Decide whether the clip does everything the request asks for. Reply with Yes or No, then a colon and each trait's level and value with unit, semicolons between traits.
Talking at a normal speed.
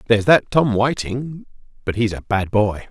Yes: average, 185 wpm